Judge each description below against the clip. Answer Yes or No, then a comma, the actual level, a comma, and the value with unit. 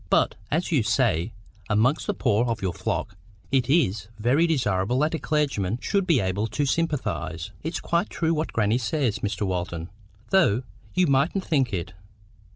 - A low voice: Yes, low, 120 Hz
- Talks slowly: No, average, 165 wpm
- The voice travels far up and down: Yes, wide, 7.3 semitones